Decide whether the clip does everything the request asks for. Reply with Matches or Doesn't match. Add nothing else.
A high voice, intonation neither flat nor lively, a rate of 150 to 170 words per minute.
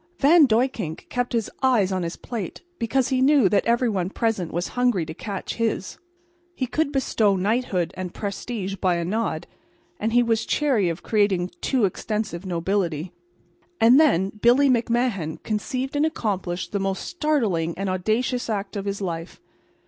Matches